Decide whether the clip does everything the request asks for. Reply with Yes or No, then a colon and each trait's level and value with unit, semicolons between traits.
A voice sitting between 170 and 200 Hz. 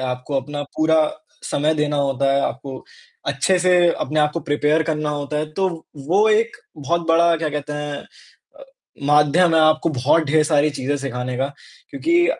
No: medium, 150 Hz